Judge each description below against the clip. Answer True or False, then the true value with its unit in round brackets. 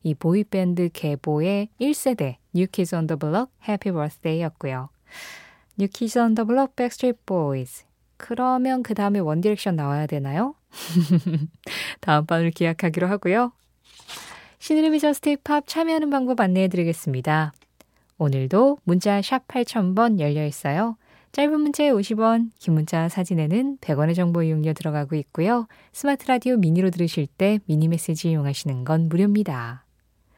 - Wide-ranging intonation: True (7.1 semitones)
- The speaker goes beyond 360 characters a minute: True (385 characters per minute)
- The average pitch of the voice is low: False (180 Hz)